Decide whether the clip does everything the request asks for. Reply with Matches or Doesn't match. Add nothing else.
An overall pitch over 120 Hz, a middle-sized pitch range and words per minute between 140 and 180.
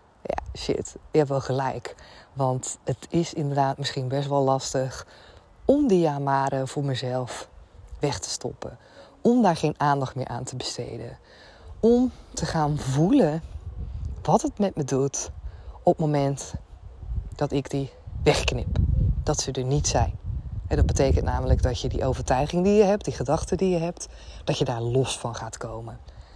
Matches